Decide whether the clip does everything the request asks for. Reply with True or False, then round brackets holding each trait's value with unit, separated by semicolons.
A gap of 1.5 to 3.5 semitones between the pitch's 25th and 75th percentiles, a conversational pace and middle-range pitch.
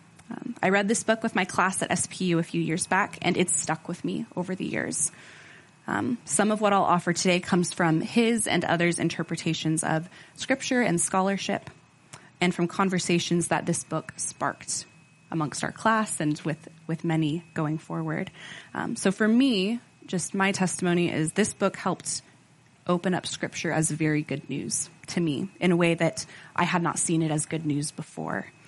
True (2.9 semitones; 185 wpm; 170 Hz)